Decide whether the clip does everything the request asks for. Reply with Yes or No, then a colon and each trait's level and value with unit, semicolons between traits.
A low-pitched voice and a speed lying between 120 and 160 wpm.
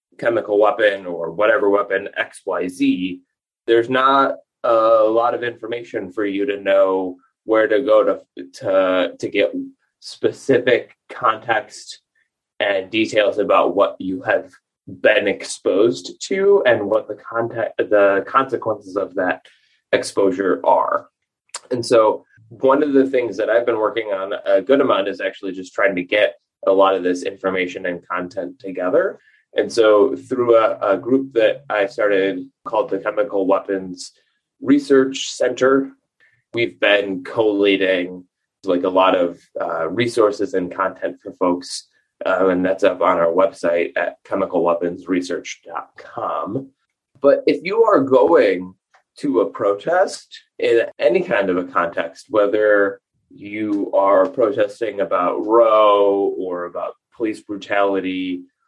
Yes: low, 105 Hz; slow, 135 wpm